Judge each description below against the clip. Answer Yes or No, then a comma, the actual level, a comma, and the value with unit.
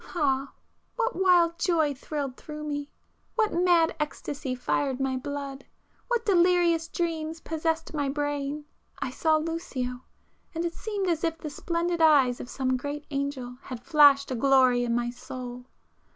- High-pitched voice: Yes, very high, 295 Hz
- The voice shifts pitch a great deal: No, average, 3.8 semitones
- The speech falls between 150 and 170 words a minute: No, average, 140 wpm